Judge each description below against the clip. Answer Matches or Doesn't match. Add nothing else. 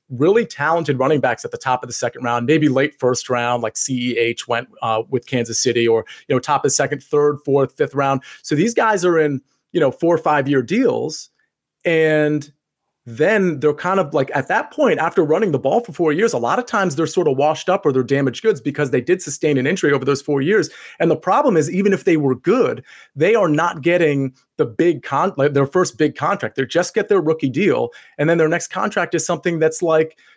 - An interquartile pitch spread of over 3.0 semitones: Matches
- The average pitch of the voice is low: Doesn't match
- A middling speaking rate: Doesn't match